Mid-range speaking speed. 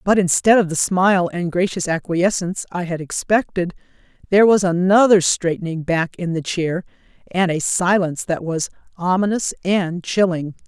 Yes: average, 150 wpm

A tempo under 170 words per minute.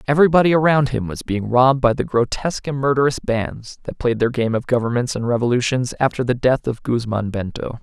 No: average, 200 wpm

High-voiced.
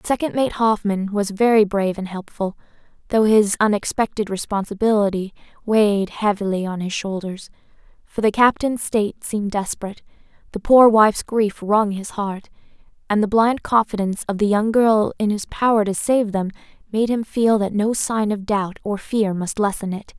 Yes: high, 210 Hz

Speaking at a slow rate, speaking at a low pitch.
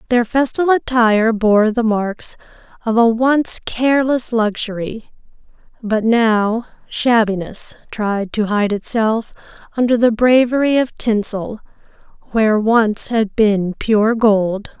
No: slow, 120 wpm; high, 225 Hz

